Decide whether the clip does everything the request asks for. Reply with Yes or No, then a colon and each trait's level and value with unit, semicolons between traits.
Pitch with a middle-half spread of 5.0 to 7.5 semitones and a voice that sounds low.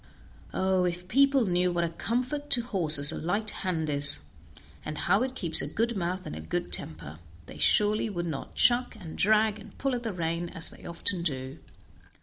No: wide, 5.4 semitones; medium, 180 Hz